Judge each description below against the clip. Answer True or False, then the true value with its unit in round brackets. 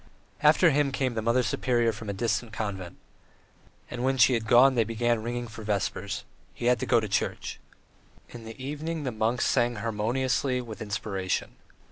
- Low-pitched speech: True (120 Hz)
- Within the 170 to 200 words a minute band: True (175 wpm)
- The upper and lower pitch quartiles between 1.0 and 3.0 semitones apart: True (2.7 semitones)